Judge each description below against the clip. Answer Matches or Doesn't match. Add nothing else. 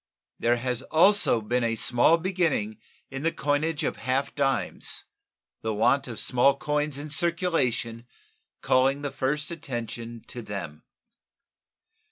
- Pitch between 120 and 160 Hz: Matches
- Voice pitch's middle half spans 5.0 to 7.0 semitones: Doesn't match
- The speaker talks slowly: Matches